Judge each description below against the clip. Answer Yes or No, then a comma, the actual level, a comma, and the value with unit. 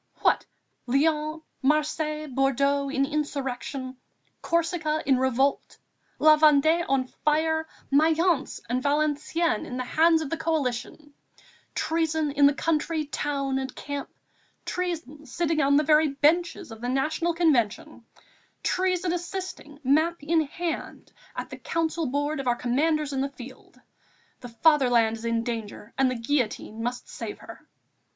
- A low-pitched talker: No, very high, 295 Hz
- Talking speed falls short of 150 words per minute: Yes, average, 140 wpm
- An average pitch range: Yes, average, 3.2 semitones